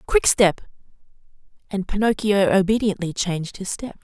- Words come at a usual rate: No, slow, 105 wpm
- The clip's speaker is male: No, female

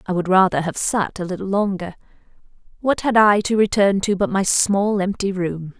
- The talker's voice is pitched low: No, high, 195 Hz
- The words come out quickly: No, average, 195 wpm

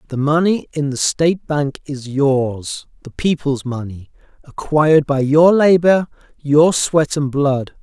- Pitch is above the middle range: No, medium, 145 Hz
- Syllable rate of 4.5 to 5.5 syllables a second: No, 3.9 syllables/s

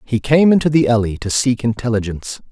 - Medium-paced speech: Yes, average, 190 wpm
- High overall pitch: No, low, 120 Hz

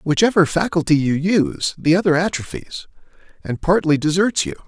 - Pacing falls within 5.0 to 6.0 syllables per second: Yes, 5.4 syllables/s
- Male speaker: Yes, male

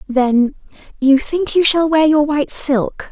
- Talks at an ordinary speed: Yes, average, 175 wpm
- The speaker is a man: No, female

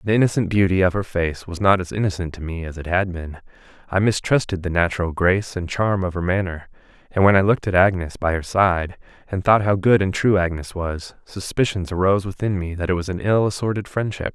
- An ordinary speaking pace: No, fast, 225 wpm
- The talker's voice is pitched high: No, very low, 95 Hz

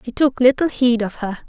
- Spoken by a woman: Yes, female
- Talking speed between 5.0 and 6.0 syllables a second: Yes, 5.4 syllables/s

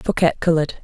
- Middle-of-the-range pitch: Yes, medium, 160 Hz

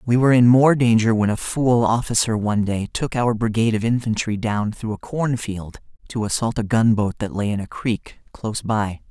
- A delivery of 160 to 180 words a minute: No, fast, 205 wpm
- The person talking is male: Yes, male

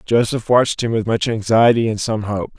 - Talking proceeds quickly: Yes, fast, 210 wpm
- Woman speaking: No, male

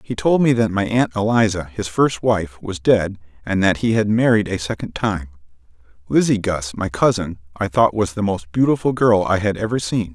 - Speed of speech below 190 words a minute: No, fast, 205 wpm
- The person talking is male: Yes, male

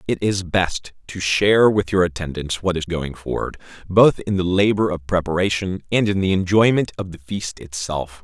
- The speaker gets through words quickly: No, average, 190 wpm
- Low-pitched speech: Yes, very low, 95 Hz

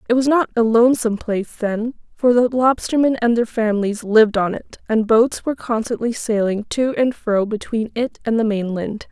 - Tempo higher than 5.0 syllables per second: Yes, 5.2 syllables/s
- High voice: Yes, high, 230 Hz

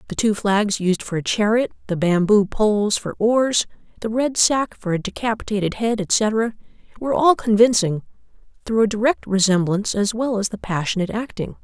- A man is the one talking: No, female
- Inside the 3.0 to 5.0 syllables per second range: No, 5.2 syllables/s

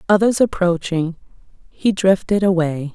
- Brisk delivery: No, slow, 100 wpm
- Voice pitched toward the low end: No, medium, 185 Hz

